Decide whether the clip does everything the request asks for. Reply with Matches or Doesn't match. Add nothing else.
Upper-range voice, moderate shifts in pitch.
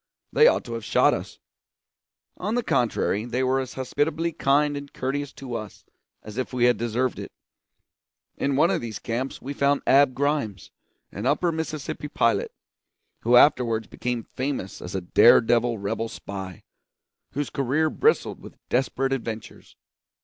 Doesn't match